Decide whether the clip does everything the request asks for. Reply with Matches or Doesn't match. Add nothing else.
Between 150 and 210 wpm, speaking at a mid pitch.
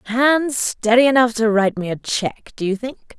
Doesn't match